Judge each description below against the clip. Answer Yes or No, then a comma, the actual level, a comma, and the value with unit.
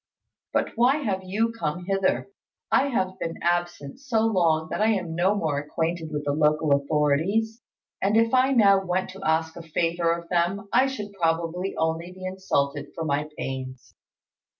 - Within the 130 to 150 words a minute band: No, average, 175 wpm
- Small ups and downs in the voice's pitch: No, average, 4.0 semitones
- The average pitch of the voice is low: No, medium, 175 Hz